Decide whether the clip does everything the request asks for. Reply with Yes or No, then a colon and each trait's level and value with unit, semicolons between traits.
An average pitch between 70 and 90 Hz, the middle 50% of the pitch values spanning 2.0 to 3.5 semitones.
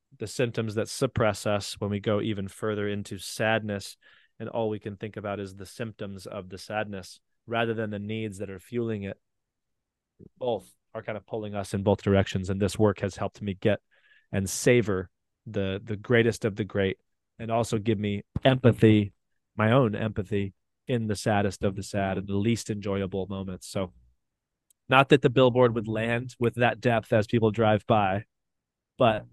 No: low, 105 Hz; narrow, 2.5 semitones